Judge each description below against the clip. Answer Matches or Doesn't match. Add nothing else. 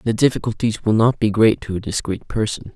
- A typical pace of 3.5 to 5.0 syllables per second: Doesn't match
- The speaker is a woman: Doesn't match